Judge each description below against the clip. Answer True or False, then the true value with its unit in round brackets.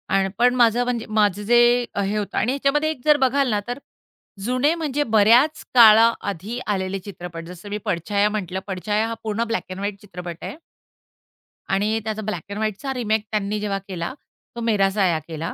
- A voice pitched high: True (215 Hz)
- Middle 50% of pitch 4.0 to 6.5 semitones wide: False (3.6 semitones)